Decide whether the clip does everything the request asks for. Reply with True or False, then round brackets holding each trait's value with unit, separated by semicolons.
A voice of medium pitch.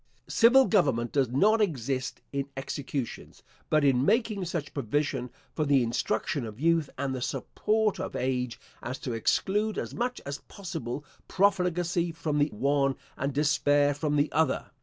True (145 Hz)